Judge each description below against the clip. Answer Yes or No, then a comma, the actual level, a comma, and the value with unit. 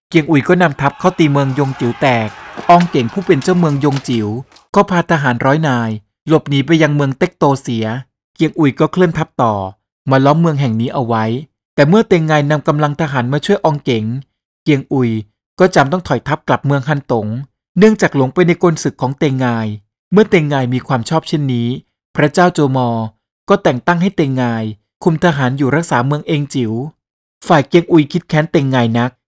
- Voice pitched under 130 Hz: No, medium, 140 Hz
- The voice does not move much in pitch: No, average, 4.8 semitones